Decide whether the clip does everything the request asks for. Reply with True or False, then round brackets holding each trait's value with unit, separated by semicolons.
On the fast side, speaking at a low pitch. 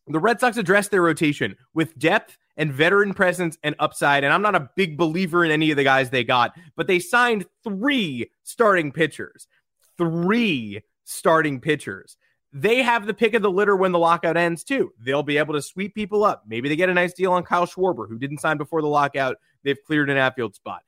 False (215 wpm; 165 Hz)